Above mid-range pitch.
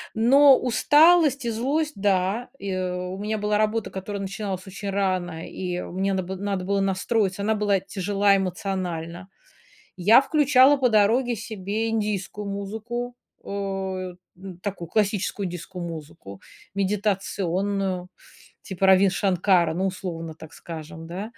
Yes: high, 195 Hz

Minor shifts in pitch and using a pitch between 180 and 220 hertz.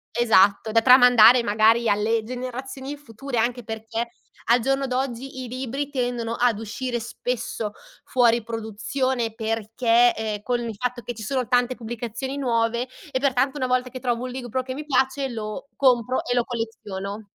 No: narrow, 2.3 semitones; high, 240 Hz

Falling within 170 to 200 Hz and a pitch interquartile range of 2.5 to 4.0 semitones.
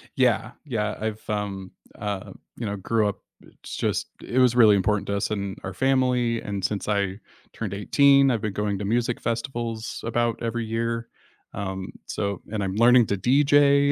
No: low, 110 Hz; average, 3.1 semitones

